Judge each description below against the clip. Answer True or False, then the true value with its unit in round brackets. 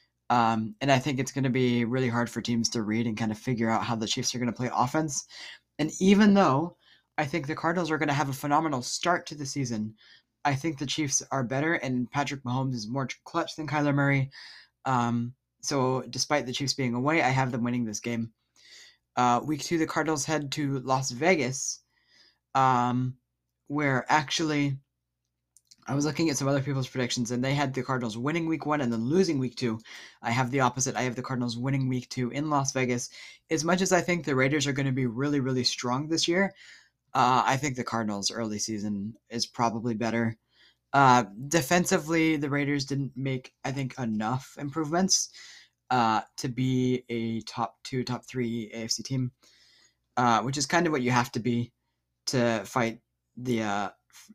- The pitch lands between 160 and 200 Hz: False (130 Hz)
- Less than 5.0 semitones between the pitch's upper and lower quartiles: True (3.4 semitones)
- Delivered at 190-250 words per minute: True (200 wpm)